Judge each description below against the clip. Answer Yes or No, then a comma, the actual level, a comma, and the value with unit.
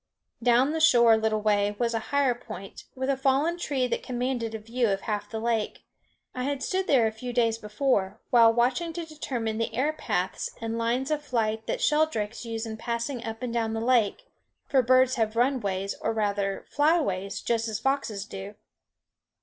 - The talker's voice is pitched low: No, high, 235 Hz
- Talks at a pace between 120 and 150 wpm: No, average, 190 wpm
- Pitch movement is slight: No, average, 3.3 semitones